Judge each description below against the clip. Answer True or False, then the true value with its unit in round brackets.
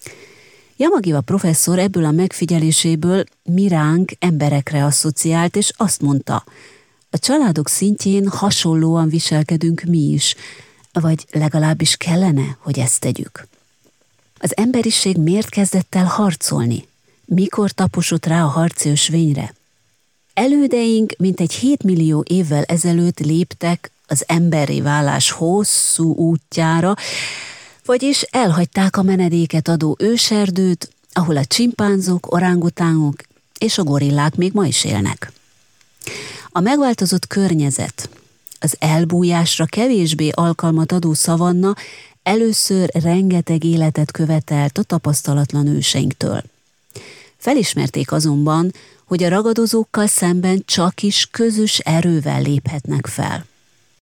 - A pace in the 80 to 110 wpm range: True (105 wpm)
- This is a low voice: False (170 Hz)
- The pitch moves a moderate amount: True (3.7 semitones)